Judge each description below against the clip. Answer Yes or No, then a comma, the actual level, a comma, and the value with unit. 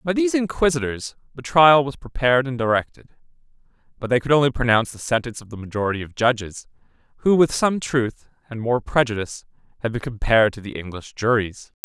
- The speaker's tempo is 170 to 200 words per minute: Yes, average, 175 wpm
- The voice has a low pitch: Yes, low, 125 Hz